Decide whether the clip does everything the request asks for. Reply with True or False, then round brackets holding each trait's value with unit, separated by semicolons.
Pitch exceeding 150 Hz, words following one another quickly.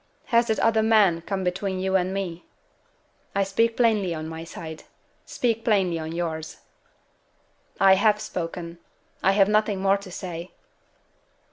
False (190 Hz; 145 wpm)